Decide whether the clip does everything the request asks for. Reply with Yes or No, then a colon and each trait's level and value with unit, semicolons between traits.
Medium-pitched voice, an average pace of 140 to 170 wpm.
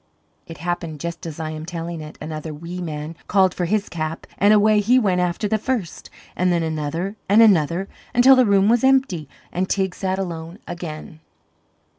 No: medium, 175 Hz; average, 185 wpm